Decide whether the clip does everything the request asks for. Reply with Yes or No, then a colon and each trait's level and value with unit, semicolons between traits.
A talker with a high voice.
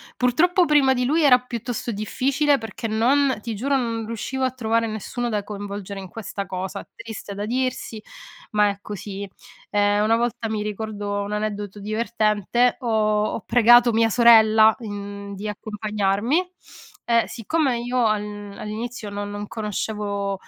Yes: high, 220 Hz